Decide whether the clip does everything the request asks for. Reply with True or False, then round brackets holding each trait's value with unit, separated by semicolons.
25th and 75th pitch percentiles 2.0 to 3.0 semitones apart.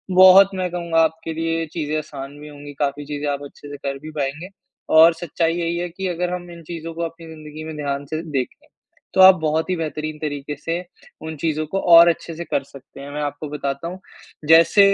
True (2.6 semitones)